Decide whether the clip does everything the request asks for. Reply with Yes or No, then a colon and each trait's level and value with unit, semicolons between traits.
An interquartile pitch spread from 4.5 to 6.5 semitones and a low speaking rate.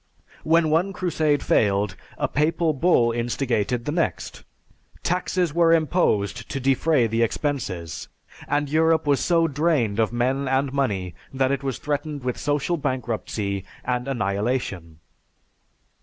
Yes: average, 5.2 semitones; slow, 130 wpm